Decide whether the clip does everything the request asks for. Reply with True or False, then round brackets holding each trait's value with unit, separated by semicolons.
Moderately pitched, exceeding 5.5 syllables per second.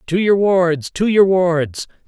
False (175 Hz; 3.4 syllables/s)